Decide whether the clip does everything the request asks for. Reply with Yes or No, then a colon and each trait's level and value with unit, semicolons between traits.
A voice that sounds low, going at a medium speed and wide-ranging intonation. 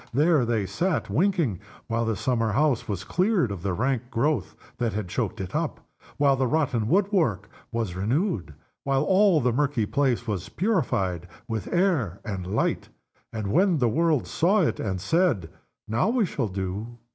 Yes: low, 120 Hz; average, 170 wpm; wide, 7.6 semitones